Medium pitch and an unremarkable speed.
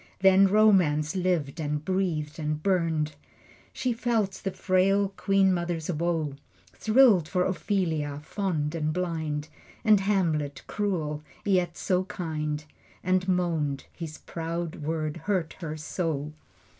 No: medium, 170 Hz; slow, 120 wpm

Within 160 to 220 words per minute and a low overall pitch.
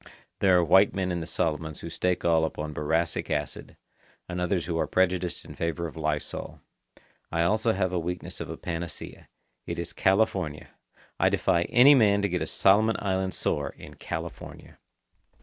Yes: average, 175 wpm; very low, 85 Hz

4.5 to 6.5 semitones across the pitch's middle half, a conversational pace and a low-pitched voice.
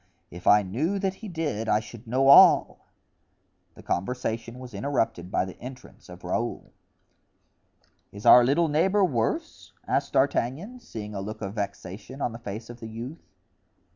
Yes: average, 5.1 semitones; average, 160 wpm; low, 115 Hz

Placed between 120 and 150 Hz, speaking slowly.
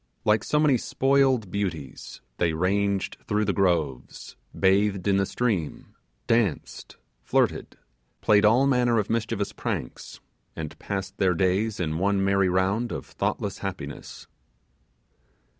No: low, 100 Hz; slow, 125 wpm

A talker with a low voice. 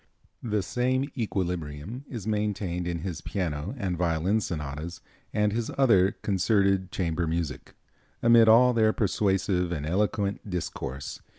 Yes: very low, 95 Hz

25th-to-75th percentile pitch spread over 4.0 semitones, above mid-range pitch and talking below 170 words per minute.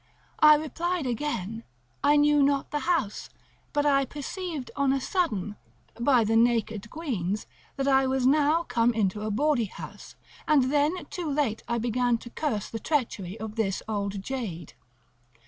Yes: average, 5.2 semitones; very high, 255 Hz; average, 160 wpm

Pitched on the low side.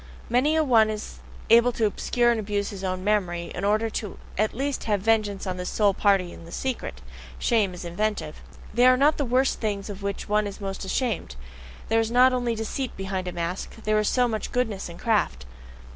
No: high, 215 Hz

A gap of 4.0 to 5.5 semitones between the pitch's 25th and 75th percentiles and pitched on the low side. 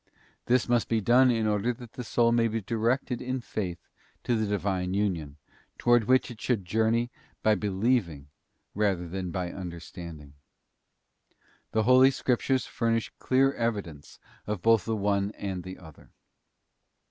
Yes: average, 4.3 semitones; low, 110 Hz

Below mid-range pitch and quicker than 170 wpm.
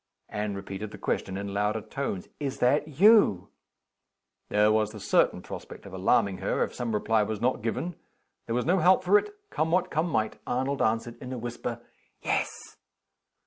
Yes: low, 115 Hz; average, 180 wpm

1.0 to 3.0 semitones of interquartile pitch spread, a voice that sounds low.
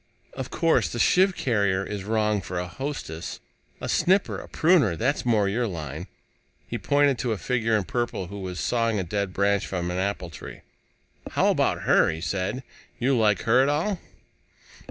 No: average, 5.3 semitones; low, 105 Hz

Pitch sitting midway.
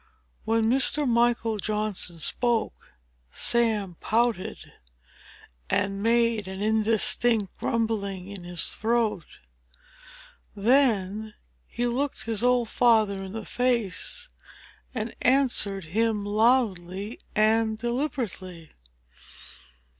No: high, 220 Hz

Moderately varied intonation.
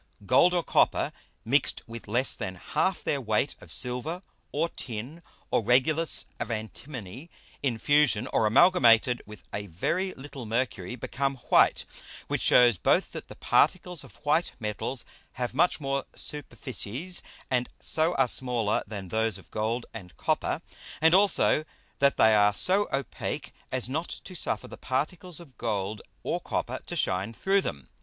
No: wide, 5.9 semitones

